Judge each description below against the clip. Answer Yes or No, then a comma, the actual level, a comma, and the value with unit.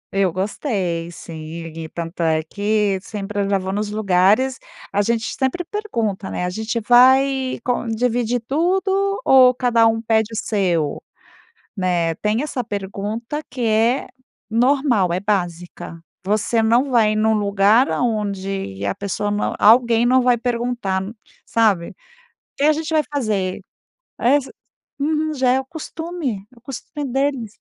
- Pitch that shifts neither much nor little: Yes, average, 4.6 semitones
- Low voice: No, high, 220 Hz